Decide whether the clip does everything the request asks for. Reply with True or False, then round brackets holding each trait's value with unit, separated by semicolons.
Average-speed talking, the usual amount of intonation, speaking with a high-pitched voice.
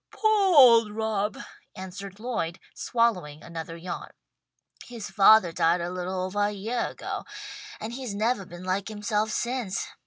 True (145 wpm; 4.0 semitones; 205 Hz)